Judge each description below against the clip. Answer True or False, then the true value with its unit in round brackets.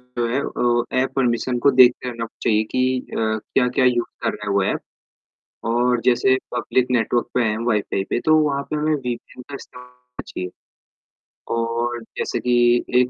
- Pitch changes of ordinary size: False (1.4 semitones)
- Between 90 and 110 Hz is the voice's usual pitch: False (125 Hz)